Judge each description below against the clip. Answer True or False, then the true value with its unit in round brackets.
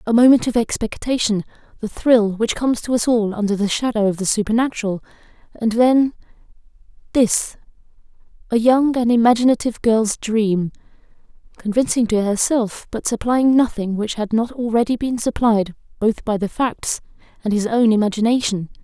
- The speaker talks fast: False (145 wpm)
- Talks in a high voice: True (225 Hz)